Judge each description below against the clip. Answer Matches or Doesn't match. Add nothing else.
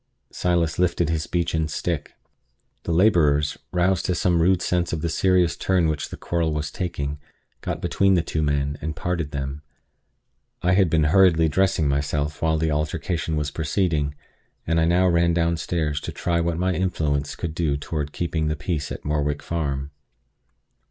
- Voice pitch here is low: Matches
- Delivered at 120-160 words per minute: Doesn't match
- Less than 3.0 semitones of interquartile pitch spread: Matches